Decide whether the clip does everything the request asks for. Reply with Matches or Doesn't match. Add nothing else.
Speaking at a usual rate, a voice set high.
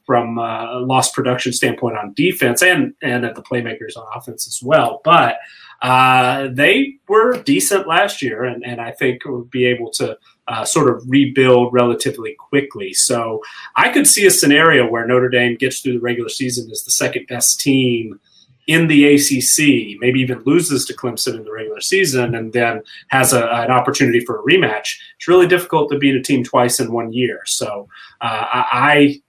Doesn't match